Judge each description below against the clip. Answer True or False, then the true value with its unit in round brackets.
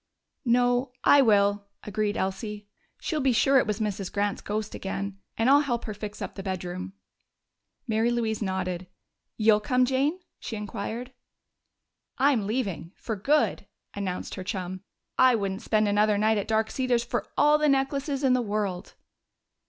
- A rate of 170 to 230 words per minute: False (160 wpm)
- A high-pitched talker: True (215 Hz)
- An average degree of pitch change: True (3.9 semitones)